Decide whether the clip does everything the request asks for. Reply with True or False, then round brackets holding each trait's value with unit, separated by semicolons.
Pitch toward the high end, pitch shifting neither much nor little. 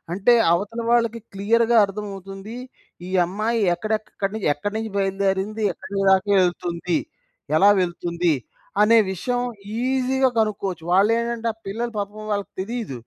True (205 Hz; 3.1 semitones)